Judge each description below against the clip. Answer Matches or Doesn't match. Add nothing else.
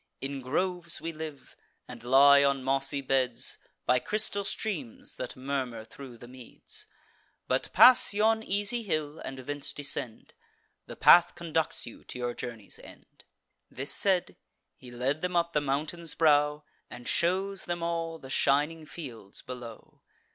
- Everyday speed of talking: Matches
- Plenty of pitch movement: Doesn't match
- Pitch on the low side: Doesn't match